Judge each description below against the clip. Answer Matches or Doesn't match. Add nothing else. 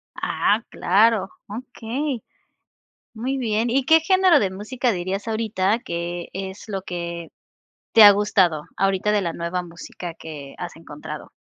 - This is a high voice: Matches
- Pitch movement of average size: Matches